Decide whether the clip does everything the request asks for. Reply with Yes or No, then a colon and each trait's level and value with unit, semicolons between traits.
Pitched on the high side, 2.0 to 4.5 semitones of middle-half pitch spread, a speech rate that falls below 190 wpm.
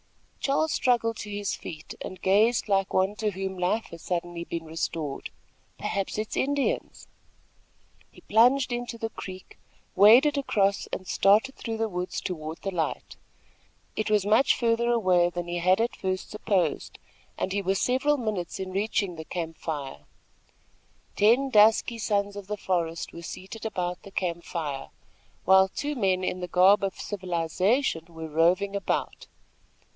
Yes: high, 195 Hz; average, 4.0 semitones; average, 160 wpm